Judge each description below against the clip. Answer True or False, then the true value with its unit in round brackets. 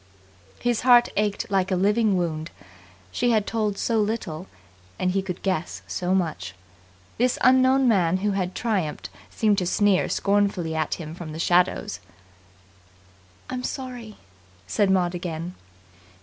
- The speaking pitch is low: False (195 Hz)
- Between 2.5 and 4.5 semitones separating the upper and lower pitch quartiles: True (3.8 semitones)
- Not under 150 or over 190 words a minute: False (140 wpm)